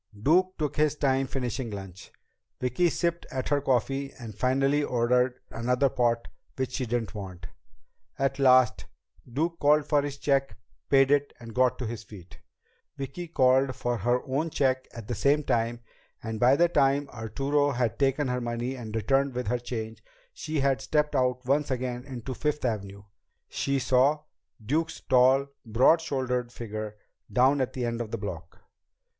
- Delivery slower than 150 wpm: No, average, 170 wpm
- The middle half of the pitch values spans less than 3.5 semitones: Yes, average, 2.9 semitones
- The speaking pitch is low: Yes, low, 130 Hz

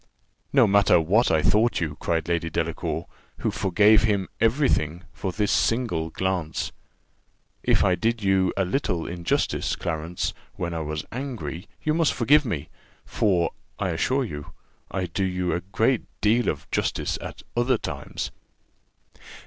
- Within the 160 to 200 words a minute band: No, average, 150 wpm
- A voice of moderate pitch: No, very low, 95 Hz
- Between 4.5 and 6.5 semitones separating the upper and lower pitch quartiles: Yes, average, 5.1 semitones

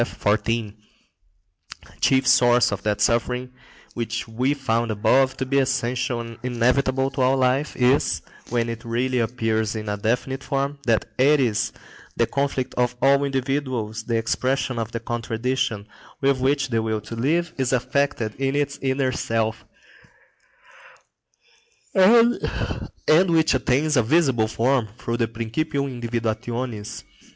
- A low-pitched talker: Yes, low, 125 Hz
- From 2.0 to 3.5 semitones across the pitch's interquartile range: Yes, average, 2.9 semitones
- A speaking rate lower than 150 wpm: Yes, slow, 135 wpm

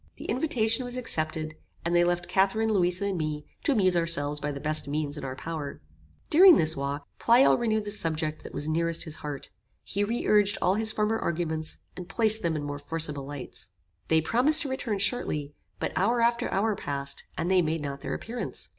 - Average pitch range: No, wide, 6.1 semitones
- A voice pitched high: No, medium, 170 Hz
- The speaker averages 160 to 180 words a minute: No, average, 200 wpm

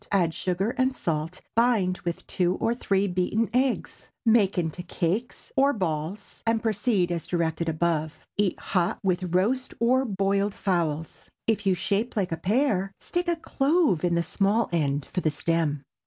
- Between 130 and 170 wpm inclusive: Yes, average, 165 wpm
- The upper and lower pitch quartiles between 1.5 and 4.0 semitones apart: No, average, 5.0 semitones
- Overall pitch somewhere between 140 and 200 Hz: Yes, high, 190 Hz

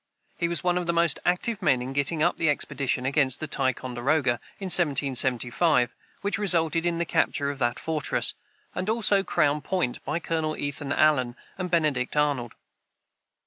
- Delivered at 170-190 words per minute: No, average, 160 wpm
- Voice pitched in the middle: Yes, medium, 150 Hz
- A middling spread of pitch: Yes, average, 4.4 semitones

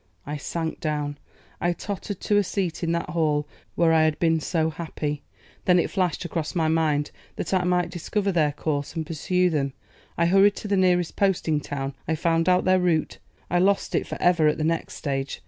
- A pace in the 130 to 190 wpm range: No, fast, 205 wpm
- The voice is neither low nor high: Yes, medium, 165 Hz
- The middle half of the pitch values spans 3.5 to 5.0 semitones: No, average, 2.9 semitones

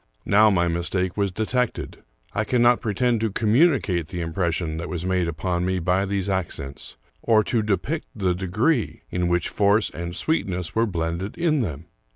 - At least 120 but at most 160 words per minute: No, average, 170 wpm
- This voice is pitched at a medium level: No, very low, 95 Hz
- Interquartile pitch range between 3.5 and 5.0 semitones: Yes, average, 4.1 semitones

